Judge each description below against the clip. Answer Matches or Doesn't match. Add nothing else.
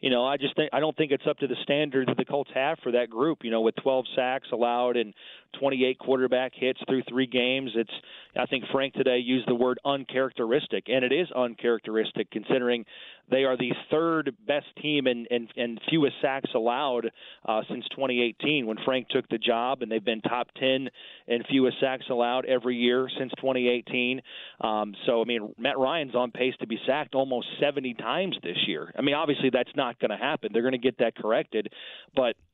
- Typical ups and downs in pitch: Doesn't match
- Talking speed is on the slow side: Doesn't match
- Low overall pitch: Matches